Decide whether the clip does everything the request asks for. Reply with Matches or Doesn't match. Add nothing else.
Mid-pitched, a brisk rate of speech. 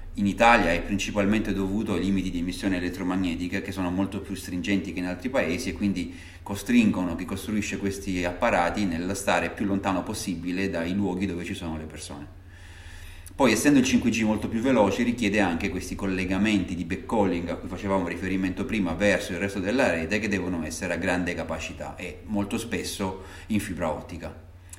Doesn't match